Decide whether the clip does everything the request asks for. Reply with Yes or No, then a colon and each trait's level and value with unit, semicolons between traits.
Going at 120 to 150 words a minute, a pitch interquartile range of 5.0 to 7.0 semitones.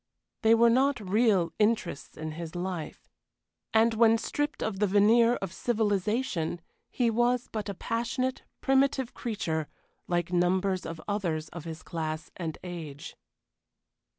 Yes: slow, 135 wpm; average, 5.3 semitones